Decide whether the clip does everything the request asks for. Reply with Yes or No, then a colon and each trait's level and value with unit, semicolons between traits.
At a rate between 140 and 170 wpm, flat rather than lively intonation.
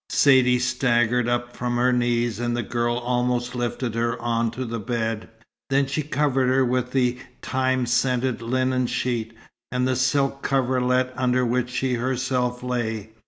Yes: average, 160 wpm; narrow, 1.2 semitones